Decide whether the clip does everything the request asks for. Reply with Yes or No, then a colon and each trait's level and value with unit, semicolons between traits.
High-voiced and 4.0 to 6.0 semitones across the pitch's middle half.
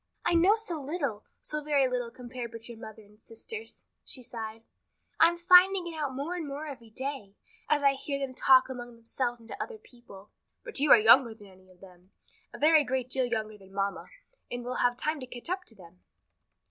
Yes: very high, 255 Hz; average, 5.0 semitones